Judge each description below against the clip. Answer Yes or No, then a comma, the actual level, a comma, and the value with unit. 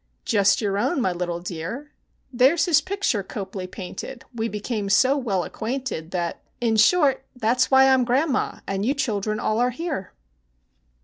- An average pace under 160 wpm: No, average, 165 wpm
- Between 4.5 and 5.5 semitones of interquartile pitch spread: Yes, average, 5.2 semitones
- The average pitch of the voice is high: Yes, high, 230 Hz